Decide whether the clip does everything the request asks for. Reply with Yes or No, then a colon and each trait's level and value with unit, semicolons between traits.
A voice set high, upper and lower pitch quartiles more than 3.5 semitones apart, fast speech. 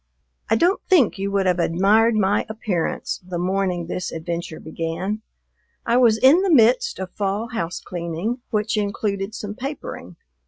No: high, 200 Hz; average, 4.3 semitones; average, 155 wpm